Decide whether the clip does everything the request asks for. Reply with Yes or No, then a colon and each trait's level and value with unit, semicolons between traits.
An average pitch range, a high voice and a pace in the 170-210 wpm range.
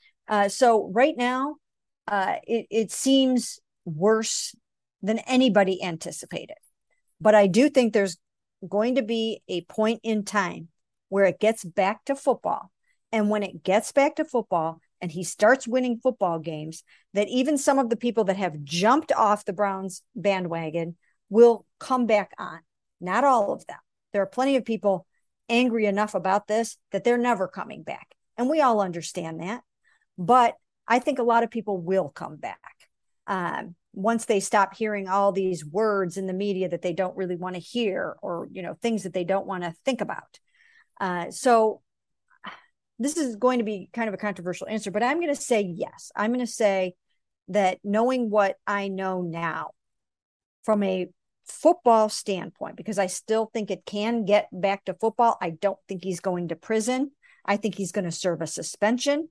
Yes: average, 3.9 semitones; high, 210 Hz; average, 180 wpm